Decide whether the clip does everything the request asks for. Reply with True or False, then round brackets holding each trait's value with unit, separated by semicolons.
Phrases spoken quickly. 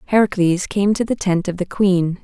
True (215 wpm)